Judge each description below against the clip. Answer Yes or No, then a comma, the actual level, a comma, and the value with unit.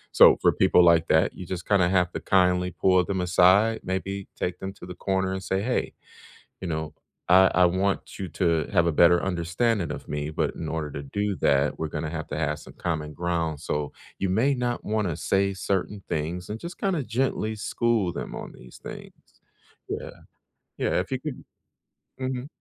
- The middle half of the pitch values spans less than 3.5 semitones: Yes, average, 3.1 semitones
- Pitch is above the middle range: No, very low, 90 Hz